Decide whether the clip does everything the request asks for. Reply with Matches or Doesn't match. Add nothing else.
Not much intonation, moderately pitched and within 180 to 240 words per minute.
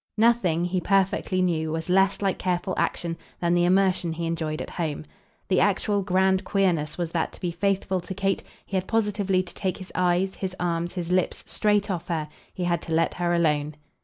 Matches